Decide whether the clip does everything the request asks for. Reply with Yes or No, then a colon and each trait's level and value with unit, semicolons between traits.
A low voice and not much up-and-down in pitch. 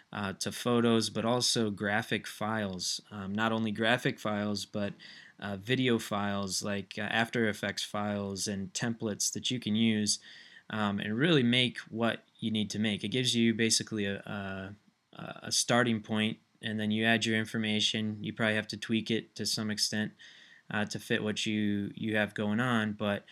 Yes: low, 110 Hz; narrow, 1.5 semitones